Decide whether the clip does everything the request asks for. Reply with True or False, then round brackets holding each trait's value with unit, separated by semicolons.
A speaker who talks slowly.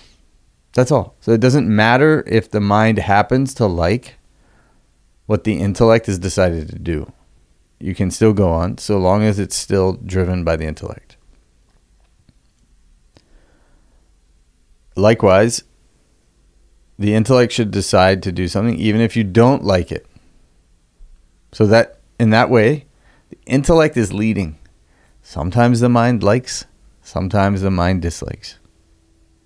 True (130 wpm)